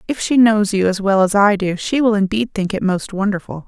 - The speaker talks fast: Yes, fast, 260 wpm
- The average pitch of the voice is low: No, high, 205 Hz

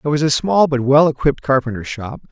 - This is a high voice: No, medium, 140 Hz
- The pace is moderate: No, fast, 235 wpm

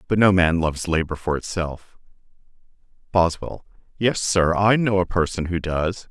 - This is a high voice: No, very low, 90 Hz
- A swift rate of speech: No, average, 155 wpm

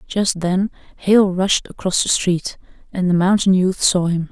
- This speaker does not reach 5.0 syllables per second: Yes, 4.2 syllables/s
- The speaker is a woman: Yes, female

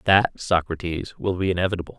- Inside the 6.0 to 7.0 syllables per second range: Yes, 6.2 syllables/s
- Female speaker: No, male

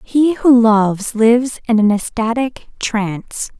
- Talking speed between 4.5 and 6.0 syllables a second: No, 3.9 syllables/s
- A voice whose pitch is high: Yes, high, 230 Hz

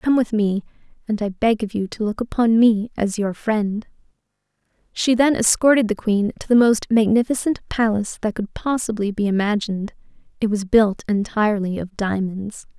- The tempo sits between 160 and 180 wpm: Yes, average, 170 wpm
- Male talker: No, female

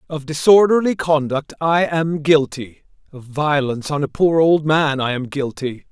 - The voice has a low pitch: No, medium, 150 Hz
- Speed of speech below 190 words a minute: Yes, average, 160 wpm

